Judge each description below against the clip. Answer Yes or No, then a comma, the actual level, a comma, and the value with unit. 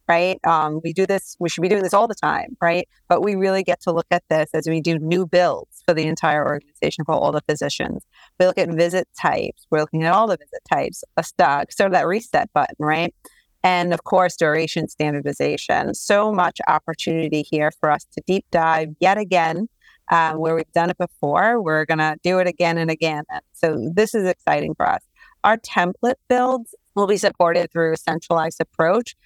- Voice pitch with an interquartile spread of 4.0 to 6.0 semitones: No, narrow, 2.6 semitones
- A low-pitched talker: No, medium, 170 Hz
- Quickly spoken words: Yes, fast, 210 wpm